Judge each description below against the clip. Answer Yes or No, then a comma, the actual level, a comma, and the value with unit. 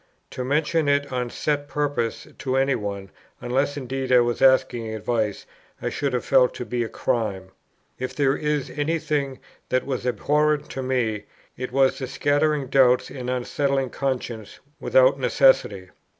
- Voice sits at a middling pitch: No, low, 130 Hz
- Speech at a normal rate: Yes, average, 160 wpm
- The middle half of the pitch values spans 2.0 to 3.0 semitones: Yes, average, 2.7 semitones